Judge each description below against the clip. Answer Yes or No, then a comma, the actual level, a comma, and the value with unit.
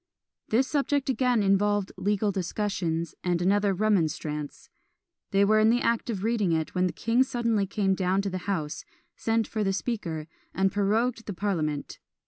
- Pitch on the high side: Yes, high, 200 Hz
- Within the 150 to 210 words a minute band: Yes, average, 165 wpm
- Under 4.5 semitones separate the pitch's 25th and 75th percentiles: Yes, average, 3.6 semitones